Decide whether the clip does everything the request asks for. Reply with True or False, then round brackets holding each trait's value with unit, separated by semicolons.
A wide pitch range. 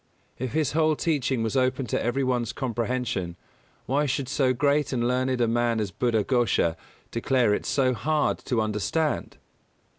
False (2.9 semitones)